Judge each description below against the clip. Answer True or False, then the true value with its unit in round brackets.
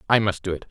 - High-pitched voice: False (100 Hz)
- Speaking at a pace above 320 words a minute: True (340 wpm)